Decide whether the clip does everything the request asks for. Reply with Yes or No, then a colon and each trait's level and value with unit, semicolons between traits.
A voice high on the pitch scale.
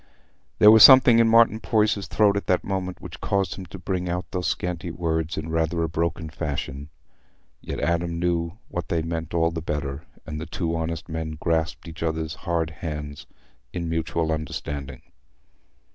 No: very low, 85 Hz